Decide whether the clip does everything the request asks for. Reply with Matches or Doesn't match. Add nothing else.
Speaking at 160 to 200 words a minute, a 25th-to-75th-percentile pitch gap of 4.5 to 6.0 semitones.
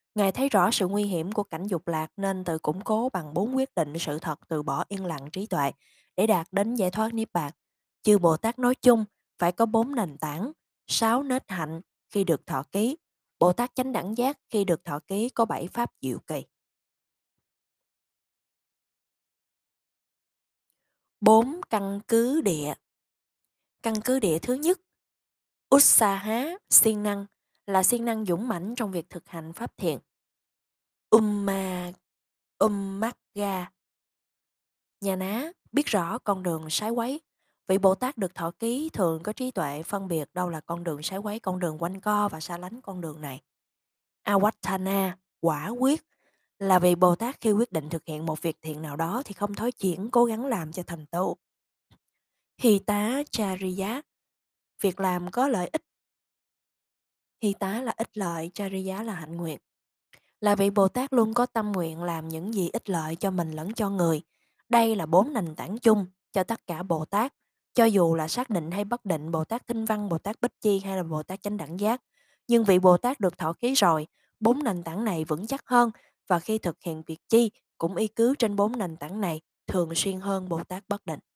Matches